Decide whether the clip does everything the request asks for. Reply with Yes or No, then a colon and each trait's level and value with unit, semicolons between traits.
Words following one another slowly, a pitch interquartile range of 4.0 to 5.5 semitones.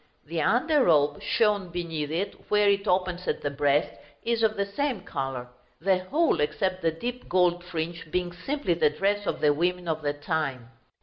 No: average, 185 wpm; average, 4.7 semitones